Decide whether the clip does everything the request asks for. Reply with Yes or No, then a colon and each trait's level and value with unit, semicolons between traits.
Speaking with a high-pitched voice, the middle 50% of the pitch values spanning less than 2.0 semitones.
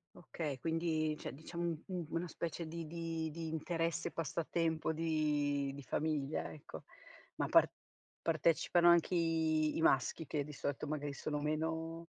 No: medium, 160 Hz; narrow, 1.6 semitones